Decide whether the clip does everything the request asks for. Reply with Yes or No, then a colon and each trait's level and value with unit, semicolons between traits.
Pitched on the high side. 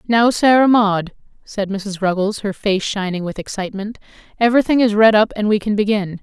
Yes: high, 210 Hz